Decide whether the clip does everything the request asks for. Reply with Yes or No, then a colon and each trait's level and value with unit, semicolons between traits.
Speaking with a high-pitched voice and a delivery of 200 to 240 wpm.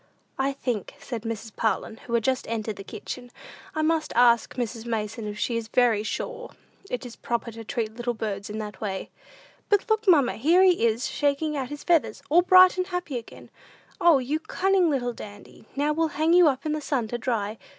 Yes: very high, 250 Hz; fast, 205 wpm